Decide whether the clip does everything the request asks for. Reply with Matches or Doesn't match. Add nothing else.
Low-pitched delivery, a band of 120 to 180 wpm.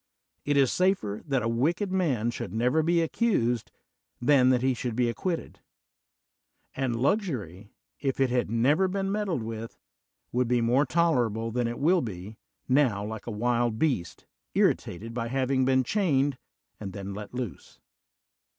Matches